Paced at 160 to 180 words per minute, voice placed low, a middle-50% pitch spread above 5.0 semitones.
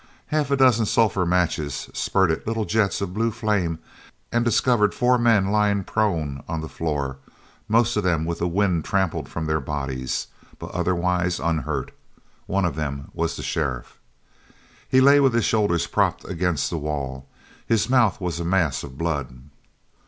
Yes: average, 165 wpm; very low, 90 Hz; wide, 5.5 semitones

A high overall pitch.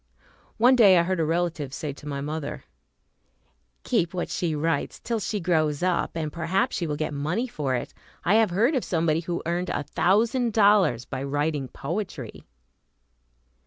No: medium, 170 Hz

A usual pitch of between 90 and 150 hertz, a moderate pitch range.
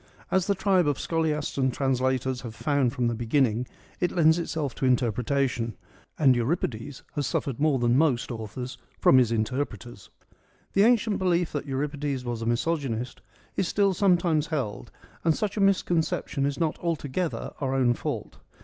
Yes: medium, 140 Hz; average, 4.9 semitones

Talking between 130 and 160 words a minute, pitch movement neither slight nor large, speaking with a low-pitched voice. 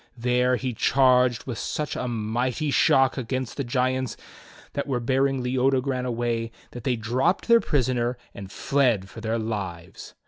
No: average, 150 wpm; narrow, 2.2 semitones; low, 125 Hz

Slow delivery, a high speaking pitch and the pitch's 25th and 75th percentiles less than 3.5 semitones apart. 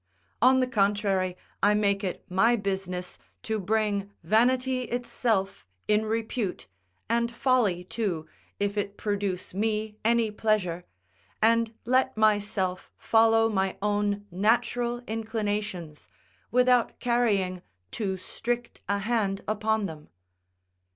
Yes: slow, 110 wpm; high, 210 Hz; average, 2.8 semitones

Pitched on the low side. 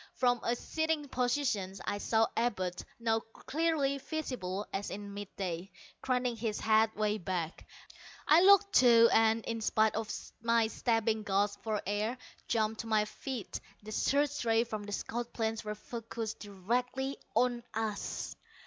No: high, 225 Hz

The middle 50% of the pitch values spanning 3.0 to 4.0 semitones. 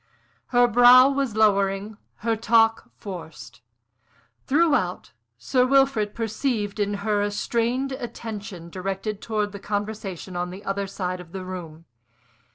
Yes: average, 3.4 semitones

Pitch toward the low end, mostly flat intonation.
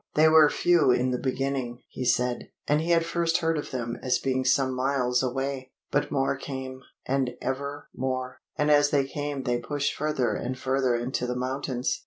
Yes: low, 130 Hz; narrow, 2.3 semitones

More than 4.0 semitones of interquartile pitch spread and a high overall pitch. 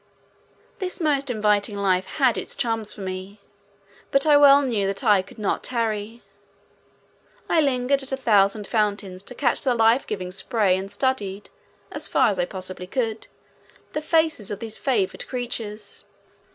Yes: average, 4.8 semitones; high, 220 Hz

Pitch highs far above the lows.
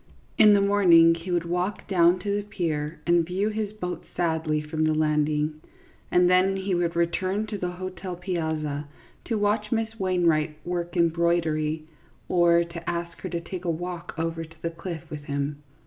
No: narrow, 2.6 semitones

